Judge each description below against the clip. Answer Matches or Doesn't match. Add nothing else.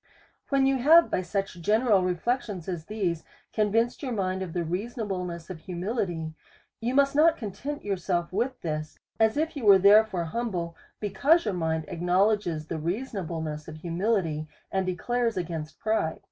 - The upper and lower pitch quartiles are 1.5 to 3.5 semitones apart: Doesn't match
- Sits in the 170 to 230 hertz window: Matches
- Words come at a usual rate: Matches